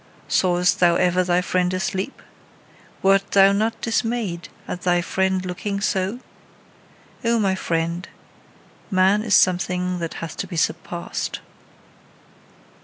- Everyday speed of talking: No, slow, 120 wpm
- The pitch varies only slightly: Yes, narrow, 1.9 semitones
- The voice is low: No, medium, 185 Hz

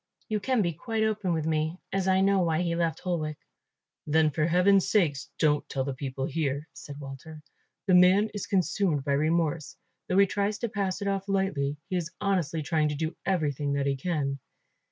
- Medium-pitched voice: Yes, medium, 165 Hz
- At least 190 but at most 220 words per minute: Yes, average, 195 wpm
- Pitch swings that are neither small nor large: Yes, average, 4.6 semitones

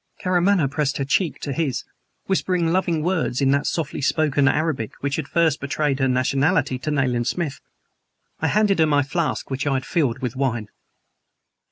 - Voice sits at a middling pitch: Yes, medium, 145 Hz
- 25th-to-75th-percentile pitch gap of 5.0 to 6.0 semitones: No, average, 3.8 semitones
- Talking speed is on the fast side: No, average, 175 wpm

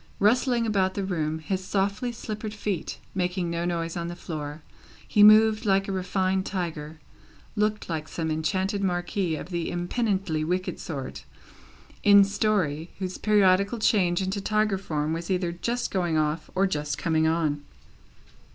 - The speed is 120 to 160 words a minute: Yes, average, 150 wpm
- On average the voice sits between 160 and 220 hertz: Yes, medium, 185 Hz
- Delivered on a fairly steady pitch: No, average, 3.6 semitones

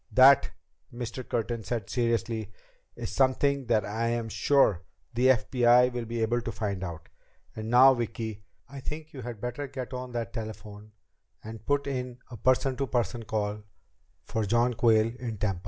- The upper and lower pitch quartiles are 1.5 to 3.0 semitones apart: Yes, narrow, 2.6 semitones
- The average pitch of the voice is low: Yes, low, 120 Hz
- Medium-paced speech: Yes, average, 170 wpm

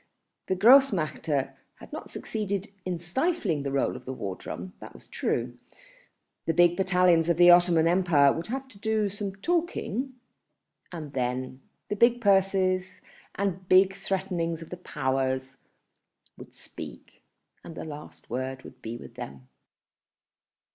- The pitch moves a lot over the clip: Yes, wide, 6.0 semitones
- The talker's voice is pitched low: No, medium, 175 Hz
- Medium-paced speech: Yes, average, 145 wpm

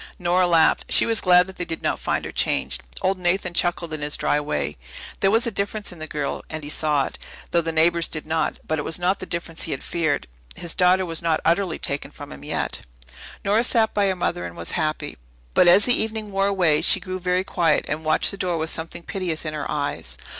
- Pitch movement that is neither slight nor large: Yes, average, 3.2 semitones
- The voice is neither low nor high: Yes, medium, 170 Hz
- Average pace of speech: No, fast, 240 wpm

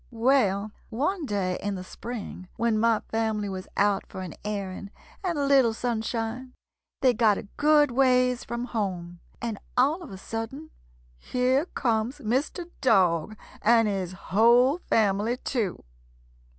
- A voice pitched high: Yes, high, 225 Hz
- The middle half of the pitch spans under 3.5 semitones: No, average, 4.0 semitones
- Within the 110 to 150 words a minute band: Yes, average, 145 wpm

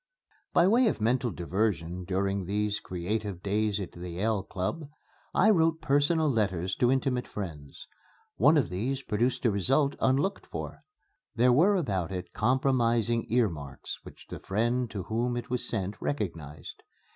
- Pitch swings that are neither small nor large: No, wide, 5.7 semitones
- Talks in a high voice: No, low, 110 Hz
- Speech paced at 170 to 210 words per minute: No, average, 150 wpm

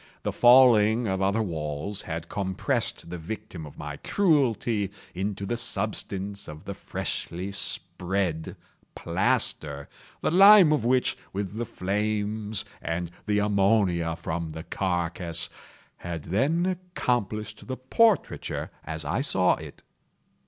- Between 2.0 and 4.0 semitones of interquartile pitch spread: No, average, 4.9 semitones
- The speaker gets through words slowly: Yes, slow, 125 wpm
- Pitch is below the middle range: Yes, low, 100 Hz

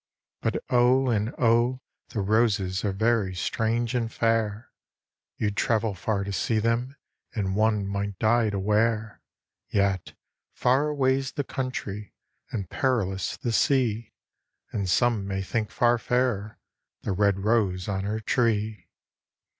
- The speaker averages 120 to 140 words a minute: Yes, slow, 135 wpm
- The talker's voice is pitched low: Yes, low, 110 Hz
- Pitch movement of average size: Yes, average, 3.0 semitones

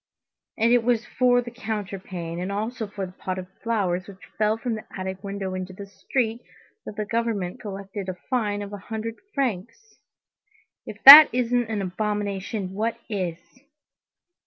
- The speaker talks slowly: No, average, 160 wpm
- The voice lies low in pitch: No, high, 205 Hz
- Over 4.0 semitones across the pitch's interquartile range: No, average, 3.5 semitones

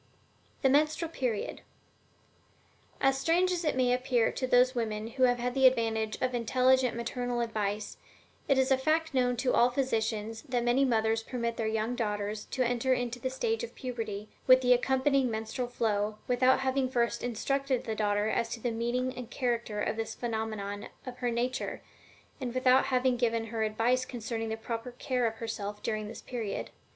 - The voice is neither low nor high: No, high, 245 Hz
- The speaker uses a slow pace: No, average, 180 wpm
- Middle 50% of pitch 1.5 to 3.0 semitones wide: Yes, narrow, 2.5 semitones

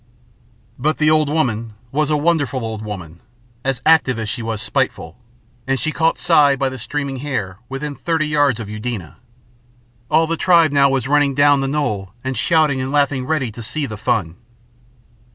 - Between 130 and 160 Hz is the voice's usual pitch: Yes, low, 135 Hz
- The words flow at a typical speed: Yes, average, 180 wpm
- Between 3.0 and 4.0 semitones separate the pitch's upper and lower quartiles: No, average, 4.9 semitones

